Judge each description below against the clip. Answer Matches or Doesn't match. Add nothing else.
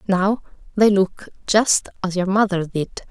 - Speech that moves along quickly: Doesn't match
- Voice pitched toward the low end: Doesn't match